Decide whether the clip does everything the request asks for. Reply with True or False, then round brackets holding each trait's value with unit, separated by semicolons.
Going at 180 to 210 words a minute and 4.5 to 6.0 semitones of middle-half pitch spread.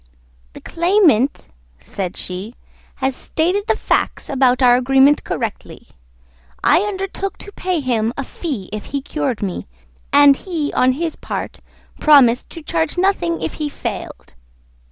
False (140 wpm; 5.5 semitones)